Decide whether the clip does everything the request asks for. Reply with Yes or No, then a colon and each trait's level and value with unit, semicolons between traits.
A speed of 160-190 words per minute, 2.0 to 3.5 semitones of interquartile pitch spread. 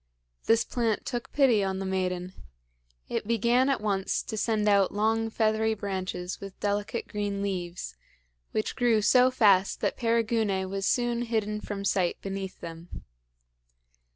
No: average, 145 wpm; average, 2.9 semitones